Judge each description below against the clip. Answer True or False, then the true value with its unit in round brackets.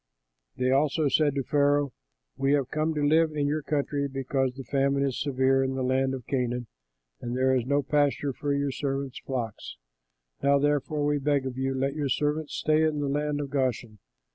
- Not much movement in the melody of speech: True (1.8 semitones)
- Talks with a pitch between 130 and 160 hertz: True (140 Hz)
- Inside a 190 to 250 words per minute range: True (195 wpm)